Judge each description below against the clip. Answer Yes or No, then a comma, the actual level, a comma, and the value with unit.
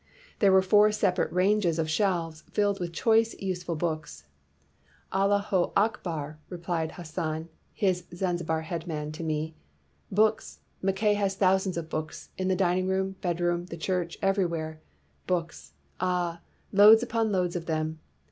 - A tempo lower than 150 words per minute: No, average, 155 wpm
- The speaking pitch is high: No, medium, 180 Hz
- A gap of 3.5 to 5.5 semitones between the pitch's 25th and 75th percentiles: No, average, 3.1 semitones